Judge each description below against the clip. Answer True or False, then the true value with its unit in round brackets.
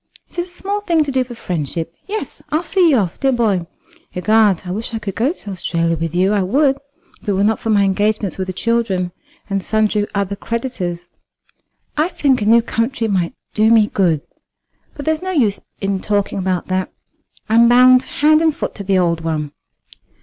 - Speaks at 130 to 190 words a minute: False (200 wpm)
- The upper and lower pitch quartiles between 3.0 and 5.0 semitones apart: False (5.6 semitones)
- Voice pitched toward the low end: False (215 Hz)